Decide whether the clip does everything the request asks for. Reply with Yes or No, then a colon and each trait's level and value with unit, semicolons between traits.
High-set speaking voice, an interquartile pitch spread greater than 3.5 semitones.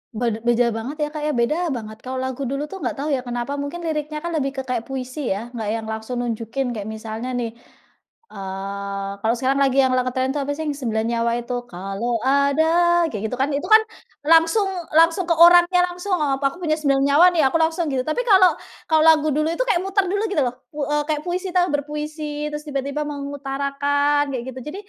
Yes: very high, 280 Hz; average, 4.3 semitones